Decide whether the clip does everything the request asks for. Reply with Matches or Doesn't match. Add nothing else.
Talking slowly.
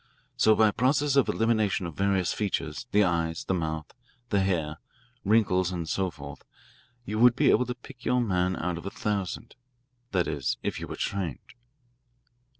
Doesn't match